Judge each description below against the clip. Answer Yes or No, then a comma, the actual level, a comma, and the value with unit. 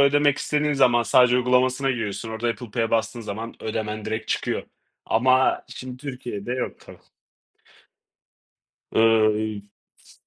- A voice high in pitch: No, low, 120 Hz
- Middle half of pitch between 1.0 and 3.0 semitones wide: Yes, average, 2.7 semitones